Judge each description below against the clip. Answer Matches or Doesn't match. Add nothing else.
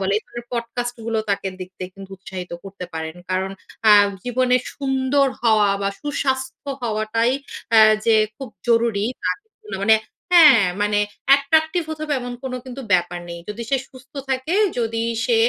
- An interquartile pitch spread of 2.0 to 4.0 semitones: Doesn't match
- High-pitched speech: Matches